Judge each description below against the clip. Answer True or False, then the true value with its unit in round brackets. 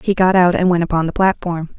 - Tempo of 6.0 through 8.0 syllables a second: True (6.1 syllables/s)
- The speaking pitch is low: False (175 Hz)